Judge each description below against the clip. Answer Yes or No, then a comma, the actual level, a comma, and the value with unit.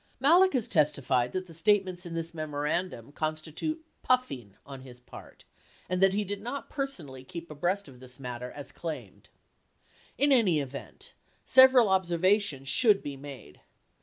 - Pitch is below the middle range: No, medium, 165 Hz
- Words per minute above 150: Yes, average, 160 wpm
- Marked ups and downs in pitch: Yes, wide, 6.8 semitones